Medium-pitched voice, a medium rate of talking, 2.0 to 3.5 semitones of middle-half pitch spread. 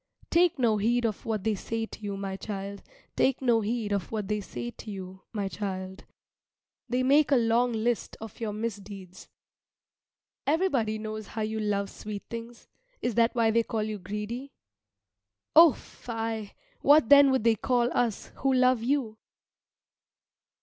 No: high, 225 Hz; average, 160 wpm; average, 2.9 semitones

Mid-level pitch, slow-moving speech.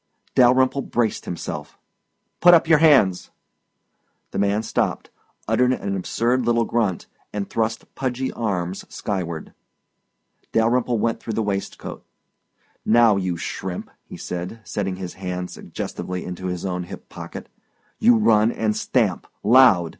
No: low, 110 Hz; slow, 130 wpm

